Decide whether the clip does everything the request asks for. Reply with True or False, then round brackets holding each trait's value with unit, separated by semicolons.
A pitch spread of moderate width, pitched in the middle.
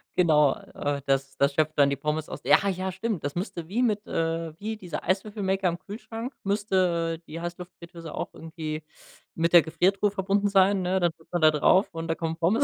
True (3.4 semitones; 175 Hz)